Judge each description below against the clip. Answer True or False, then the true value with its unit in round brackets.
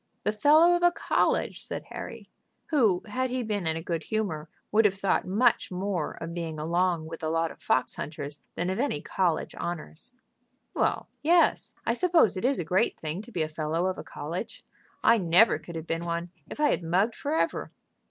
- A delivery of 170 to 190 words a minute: False (200 wpm)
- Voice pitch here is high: False (180 Hz)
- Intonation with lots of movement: True (5.7 semitones)